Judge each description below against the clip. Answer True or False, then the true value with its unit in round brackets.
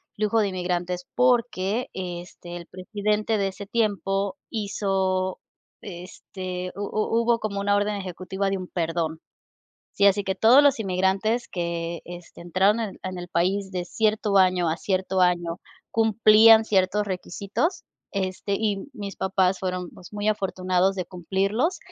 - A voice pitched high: True (195 Hz)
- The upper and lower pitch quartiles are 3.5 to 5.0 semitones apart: False (2.5 semitones)